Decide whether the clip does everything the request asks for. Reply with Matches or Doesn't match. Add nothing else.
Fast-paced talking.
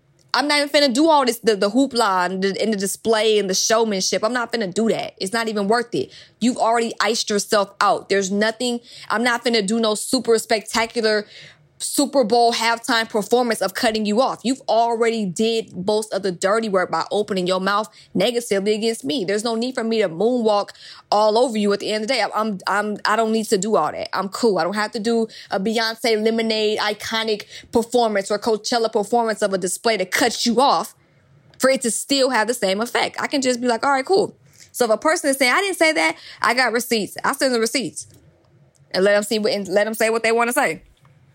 Matches